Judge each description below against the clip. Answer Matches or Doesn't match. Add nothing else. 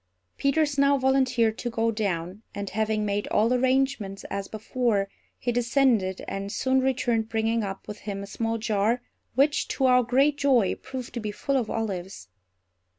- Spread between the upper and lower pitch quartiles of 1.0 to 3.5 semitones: Doesn't match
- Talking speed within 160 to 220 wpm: Matches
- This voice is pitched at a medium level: Doesn't match